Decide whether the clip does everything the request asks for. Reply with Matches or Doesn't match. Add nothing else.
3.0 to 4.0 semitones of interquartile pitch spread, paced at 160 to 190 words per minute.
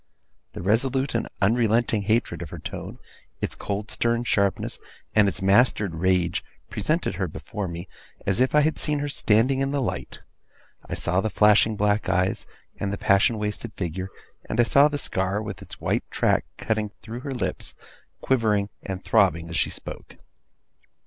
Matches